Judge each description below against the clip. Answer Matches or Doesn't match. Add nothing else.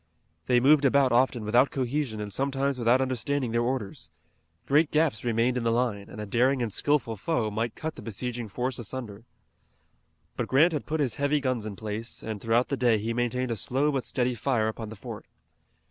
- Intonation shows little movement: Doesn't match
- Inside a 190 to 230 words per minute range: Matches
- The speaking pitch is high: Doesn't match